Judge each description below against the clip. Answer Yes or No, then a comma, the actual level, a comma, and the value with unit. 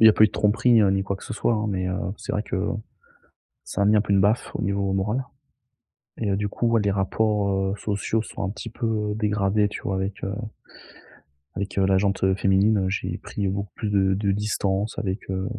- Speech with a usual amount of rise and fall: No, narrow, 1.7 semitones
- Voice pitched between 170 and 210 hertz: No, low, 100 Hz